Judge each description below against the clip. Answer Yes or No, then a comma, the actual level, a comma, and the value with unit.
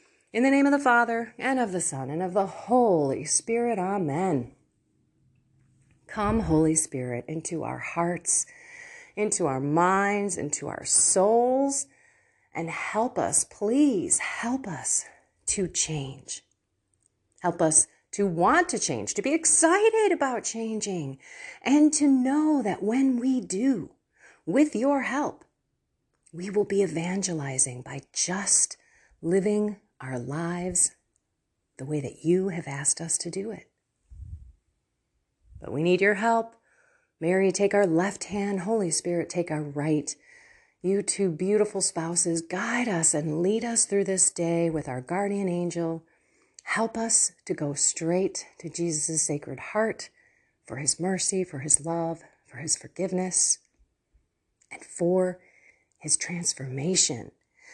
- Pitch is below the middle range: No, medium, 180 Hz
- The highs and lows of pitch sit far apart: Yes, wide, 6.7 semitones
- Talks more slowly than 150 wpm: Yes, slow, 135 wpm